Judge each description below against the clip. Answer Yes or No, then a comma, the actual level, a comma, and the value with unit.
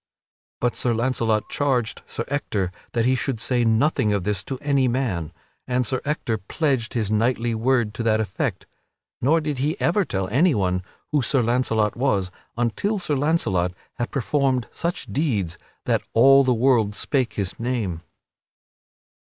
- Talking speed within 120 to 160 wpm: Yes, average, 155 wpm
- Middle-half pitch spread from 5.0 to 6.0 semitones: No, average, 4.0 semitones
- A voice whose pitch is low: Yes, low, 120 Hz